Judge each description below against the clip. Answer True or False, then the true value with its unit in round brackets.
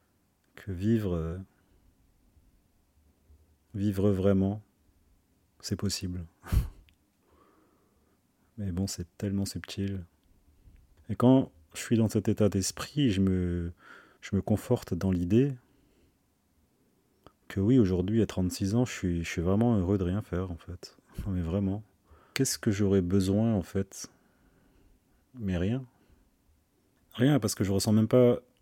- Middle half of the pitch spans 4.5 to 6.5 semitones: False (3.1 semitones)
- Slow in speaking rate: True (130 wpm)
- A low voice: True (95 Hz)